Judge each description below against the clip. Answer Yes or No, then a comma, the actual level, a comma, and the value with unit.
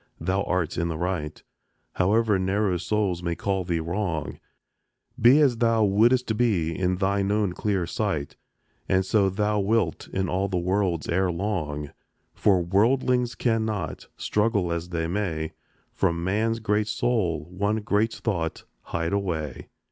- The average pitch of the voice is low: Yes, very low, 95 Hz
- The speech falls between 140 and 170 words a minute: Yes, average, 145 wpm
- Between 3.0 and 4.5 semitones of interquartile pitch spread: Yes, average, 3.8 semitones